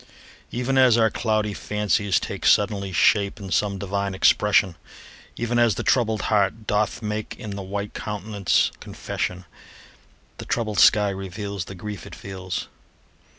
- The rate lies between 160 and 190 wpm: No, average, 145 wpm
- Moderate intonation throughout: No, narrow, 1.8 semitones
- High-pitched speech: No, low, 105 Hz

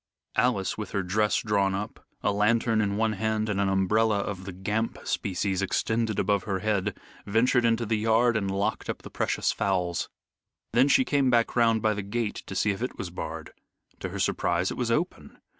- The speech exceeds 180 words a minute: Yes, average, 200 wpm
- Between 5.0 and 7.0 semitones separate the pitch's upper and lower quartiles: No, narrow, 2.6 semitones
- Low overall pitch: Yes, low, 105 Hz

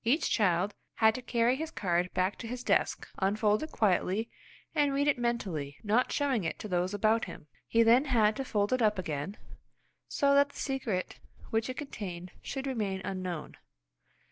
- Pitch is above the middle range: Yes, high, 220 Hz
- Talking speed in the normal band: Yes, average, 180 wpm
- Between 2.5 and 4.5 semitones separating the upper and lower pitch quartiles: No, wide, 5.4 semitones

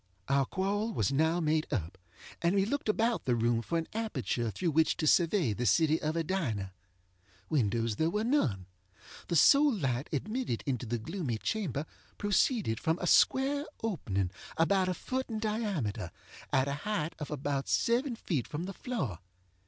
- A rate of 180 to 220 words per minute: No, average, 170 wpm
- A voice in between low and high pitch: Yes, medium, 160 Hz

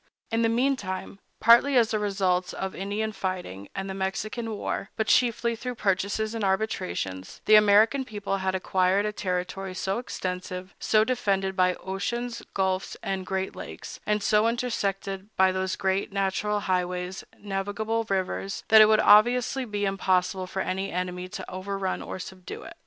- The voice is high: Yes, high, 195 Hz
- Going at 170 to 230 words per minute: No, average, 160 wpm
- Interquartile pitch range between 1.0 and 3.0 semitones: Yes, narrow, 2.5 semitones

